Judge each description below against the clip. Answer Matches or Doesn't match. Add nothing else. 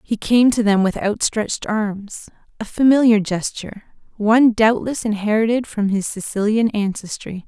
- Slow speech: Matches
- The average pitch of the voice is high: Matches